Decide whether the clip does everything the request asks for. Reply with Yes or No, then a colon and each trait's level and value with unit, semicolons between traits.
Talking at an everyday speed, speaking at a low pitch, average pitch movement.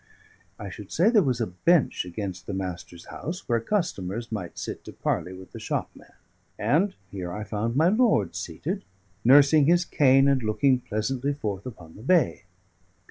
No: average, 170 wpm; low, 115 Hz; wide, 7.5 semitones